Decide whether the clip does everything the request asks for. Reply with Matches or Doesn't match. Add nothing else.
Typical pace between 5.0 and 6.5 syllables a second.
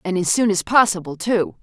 Matches